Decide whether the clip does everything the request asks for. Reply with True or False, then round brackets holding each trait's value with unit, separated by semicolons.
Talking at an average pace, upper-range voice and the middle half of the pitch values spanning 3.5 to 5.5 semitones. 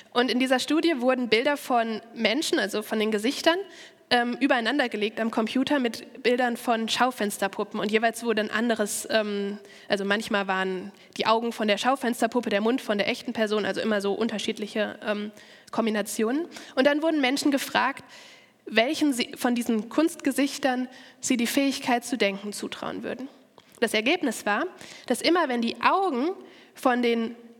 True (160 wpm; 235 Hz; 4.1 semitones)